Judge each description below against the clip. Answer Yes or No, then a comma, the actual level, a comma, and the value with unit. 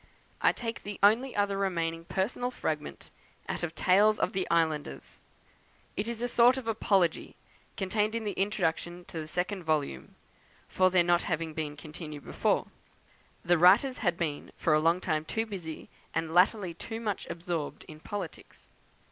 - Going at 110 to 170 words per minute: Yes, average, 165 wpm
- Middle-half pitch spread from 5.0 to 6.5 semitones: No, average, 4.3 semitones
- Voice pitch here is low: No, medium, 180 Hz